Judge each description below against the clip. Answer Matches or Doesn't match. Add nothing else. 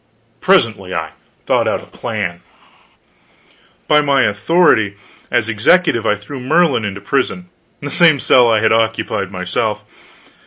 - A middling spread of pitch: Doesn't match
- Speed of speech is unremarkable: Doesn't match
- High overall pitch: Doesn't match